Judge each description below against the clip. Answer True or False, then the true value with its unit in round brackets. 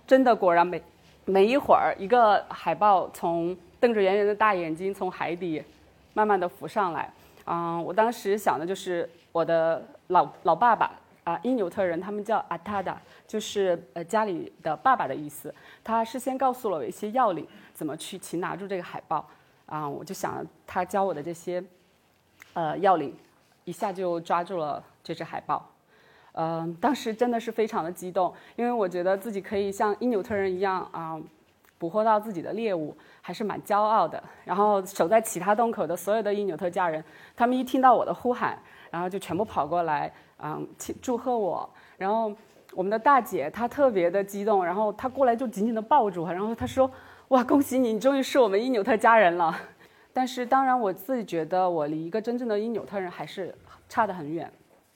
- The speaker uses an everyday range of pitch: True (4.6 semitones)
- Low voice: False (200 Hz)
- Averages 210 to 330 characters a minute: True (290 characters per minute)